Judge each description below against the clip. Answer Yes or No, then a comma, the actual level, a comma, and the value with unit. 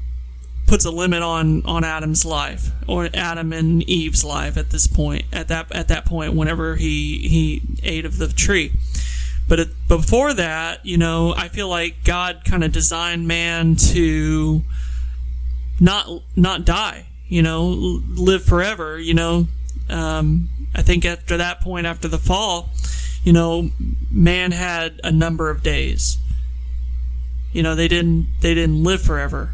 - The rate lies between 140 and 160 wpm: Yes, average, 155 wpm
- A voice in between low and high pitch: Yes, medium, 155 Hz